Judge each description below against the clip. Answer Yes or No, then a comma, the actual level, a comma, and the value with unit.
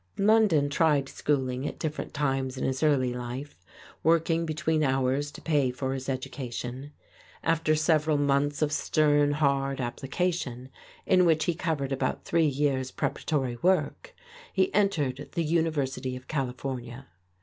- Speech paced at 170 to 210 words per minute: No, average, 140 wpm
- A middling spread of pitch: Yes, average, 3.2 semitones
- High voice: No, medium, 145 Hz